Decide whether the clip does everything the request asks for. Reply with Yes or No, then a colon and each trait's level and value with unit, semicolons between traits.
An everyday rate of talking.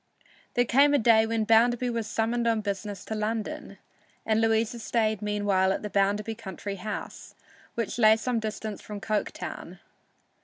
Yes: average, 155 wpm